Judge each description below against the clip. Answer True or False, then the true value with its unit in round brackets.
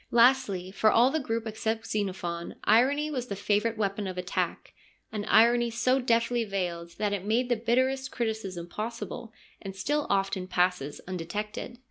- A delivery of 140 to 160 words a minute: True (155 wpm)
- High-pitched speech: True (220 Hz)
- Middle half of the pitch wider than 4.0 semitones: False (3.7 semitones)